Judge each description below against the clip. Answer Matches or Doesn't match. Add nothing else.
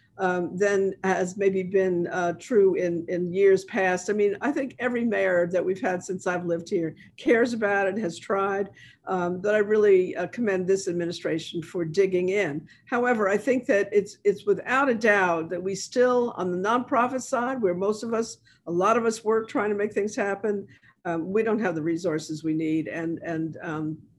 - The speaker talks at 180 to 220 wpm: Matches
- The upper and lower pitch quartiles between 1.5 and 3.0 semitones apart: Doesn't match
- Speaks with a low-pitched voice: Doesn't match